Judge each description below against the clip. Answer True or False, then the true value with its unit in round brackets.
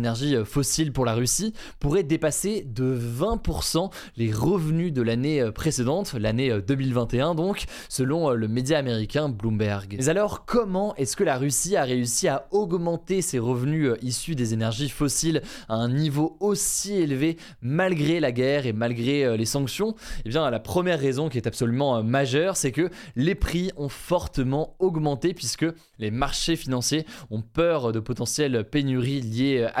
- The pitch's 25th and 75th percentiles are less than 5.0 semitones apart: False (5.3 semitones)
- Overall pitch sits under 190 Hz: True (140 Hz)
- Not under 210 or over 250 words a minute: False (155 wpm)